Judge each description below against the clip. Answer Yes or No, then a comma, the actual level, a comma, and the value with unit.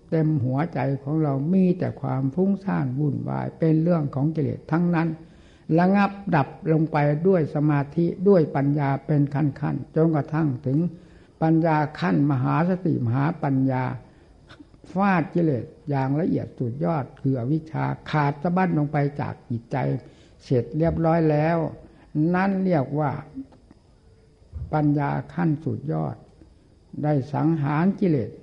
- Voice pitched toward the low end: No, medium, 150 Hz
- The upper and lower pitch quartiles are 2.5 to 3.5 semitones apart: Yes, average, 3.1 semitones